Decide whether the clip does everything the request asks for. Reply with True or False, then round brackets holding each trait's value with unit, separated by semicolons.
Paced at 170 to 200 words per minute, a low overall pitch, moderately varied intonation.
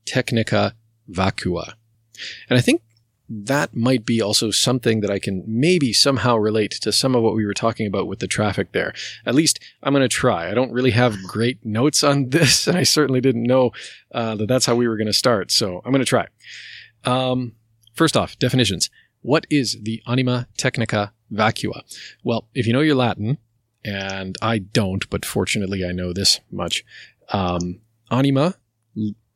True (180 wpm; 115 Hz; 3.2 semitones)